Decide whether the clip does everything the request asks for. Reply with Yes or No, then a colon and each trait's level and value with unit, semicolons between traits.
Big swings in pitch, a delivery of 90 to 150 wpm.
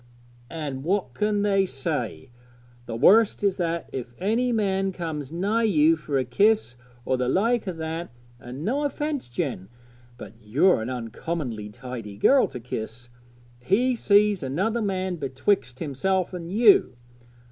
Yes: wide, 8.0 semitones; average, 145 wpm